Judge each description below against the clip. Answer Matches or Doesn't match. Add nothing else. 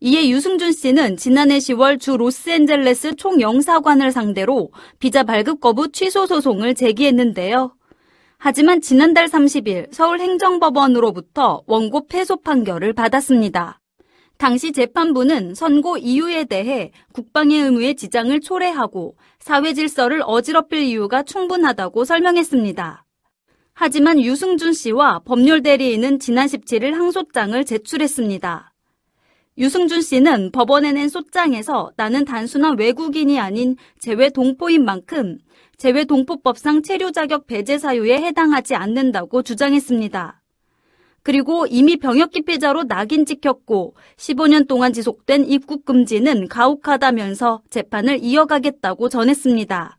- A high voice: Matches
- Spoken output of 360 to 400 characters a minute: Doesn't match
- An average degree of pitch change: Matches